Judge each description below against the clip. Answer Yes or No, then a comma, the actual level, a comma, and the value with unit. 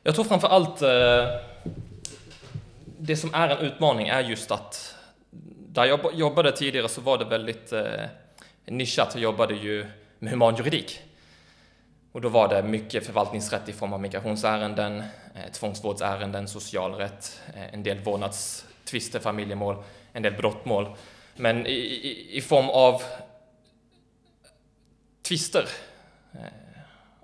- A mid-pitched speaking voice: No, low, 110 Hz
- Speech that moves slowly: Yes, slow, 110 wpm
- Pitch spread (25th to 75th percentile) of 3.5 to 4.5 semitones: Yes, average, 4.1 semitones